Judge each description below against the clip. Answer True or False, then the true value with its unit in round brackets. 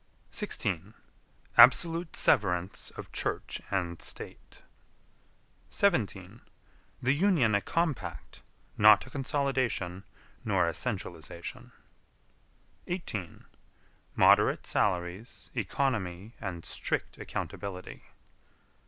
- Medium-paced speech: False (80 wpm)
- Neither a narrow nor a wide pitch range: False (6.9 semitones)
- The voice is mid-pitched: False (105 Hz)